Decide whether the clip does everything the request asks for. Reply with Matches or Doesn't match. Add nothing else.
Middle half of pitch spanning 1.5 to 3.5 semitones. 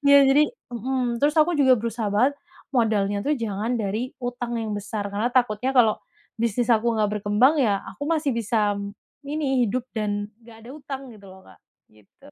Doesn't match